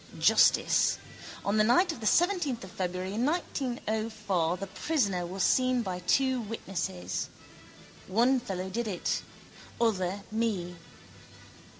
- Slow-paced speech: Yes, slow, 115 wpm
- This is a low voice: No, high, 215 Hz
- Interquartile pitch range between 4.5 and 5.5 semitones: Yes, average, 5.0 semitones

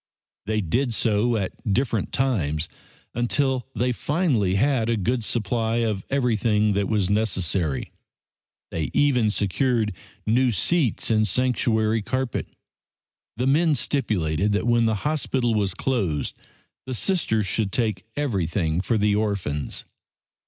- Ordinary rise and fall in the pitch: Yes, average, 4.1 semitones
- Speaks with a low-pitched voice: Yes, low, 110 Hz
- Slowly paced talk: Yes, slow, 125 wpm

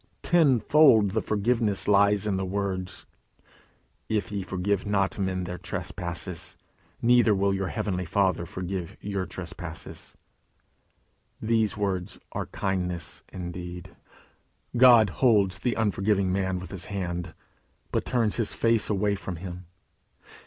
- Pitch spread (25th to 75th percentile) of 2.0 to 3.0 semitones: Yes, narrow, 2.6 semitones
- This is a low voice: Yes, low, 100 Hz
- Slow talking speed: Yes, slow, 125 wpm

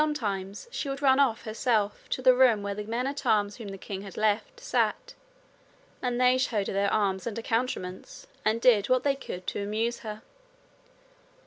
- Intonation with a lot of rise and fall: No, average, 4.0 semitones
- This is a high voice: Yes, high, 225 Hz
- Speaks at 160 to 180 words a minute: No, average, 190 wpm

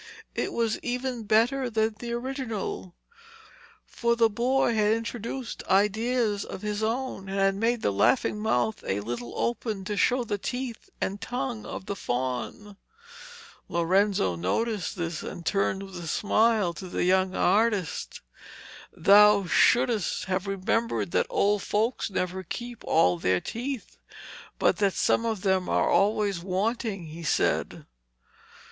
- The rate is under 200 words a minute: Yes, average, 145 wpm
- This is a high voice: Yes, high, 210 Hz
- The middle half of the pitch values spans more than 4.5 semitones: No, average, 3.7 semitones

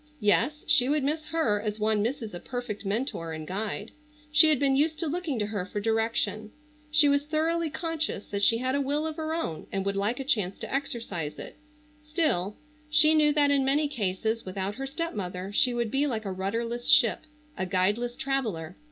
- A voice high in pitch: Yes, high, 240 Hz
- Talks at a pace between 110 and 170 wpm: No, average, 200 wpm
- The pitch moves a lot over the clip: Yes, wide, 6.5 semitones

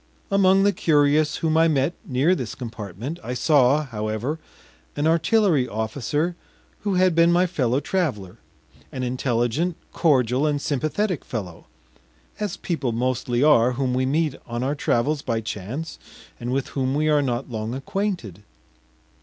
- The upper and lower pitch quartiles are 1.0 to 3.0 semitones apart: No, average, 5.1 semitones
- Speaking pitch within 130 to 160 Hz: Yes, medium, 140 Hz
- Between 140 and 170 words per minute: Yes, average, 145 wpm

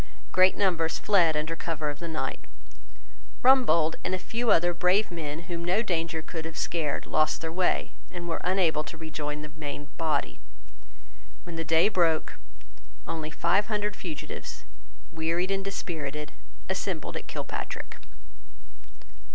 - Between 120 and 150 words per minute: Yes, average, 145 wpm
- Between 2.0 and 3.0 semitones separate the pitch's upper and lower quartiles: Yes, average, 2.7 semitones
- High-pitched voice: No, medium, 165 Hz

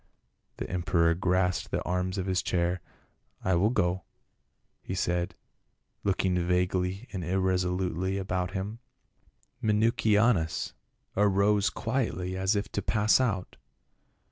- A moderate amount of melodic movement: No, narrow, 2.1 semitones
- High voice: No, very low, 95 Hz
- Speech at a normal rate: No, slow, 115 wpm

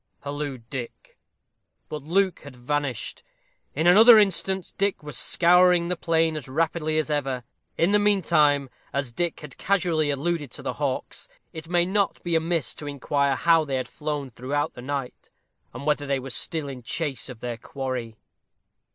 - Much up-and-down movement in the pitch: No, average, 4.0 semitones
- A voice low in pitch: No, medium, 150 Hz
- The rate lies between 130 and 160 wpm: No, average, 170 wpm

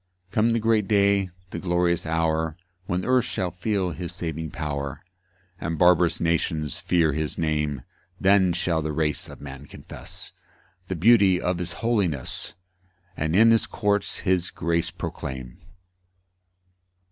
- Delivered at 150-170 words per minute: No, average, 140 wpm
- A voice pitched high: No, very low, 85 Hz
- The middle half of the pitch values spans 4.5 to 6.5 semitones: No, average, 3.7 semitones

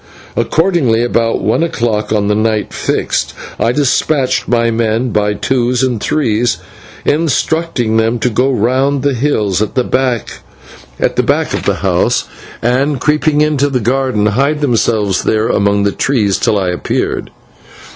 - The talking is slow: No, average, 145 wpm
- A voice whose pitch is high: No, low, 120 Hz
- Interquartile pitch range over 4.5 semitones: No, average, 4.1 semitones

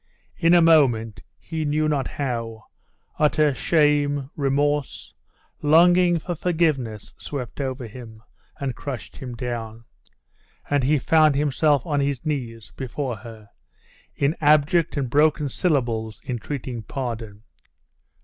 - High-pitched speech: No, medium, 140 Hz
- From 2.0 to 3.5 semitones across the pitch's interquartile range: No, average, 4.2 semitones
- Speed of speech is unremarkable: No, slow, 120 wpm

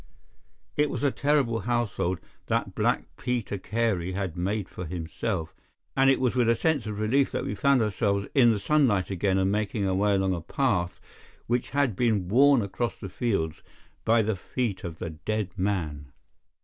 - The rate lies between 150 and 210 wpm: Yes, average, 180 wpm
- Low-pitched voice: Yes, low, 105 Hz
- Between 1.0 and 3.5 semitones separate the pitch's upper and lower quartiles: No, average, 4.5 semitones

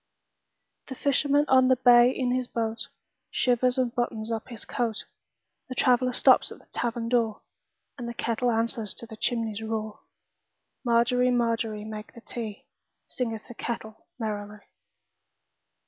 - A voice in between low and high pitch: No, high, 235 Hz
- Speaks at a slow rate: Yes, slow, 120 wpm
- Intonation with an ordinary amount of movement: No, narrow, 2.0 semitones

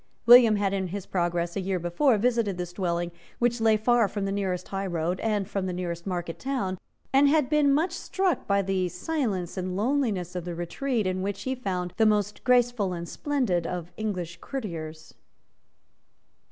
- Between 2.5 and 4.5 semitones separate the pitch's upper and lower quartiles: No, average, 5.1 semitones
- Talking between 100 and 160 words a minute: No, average, 180 wpm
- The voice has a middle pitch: No, high, 195 Hz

